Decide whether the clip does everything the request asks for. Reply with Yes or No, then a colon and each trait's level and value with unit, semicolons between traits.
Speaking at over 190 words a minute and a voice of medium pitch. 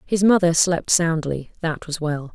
No: average, 180 wpm; medium, 165 Hz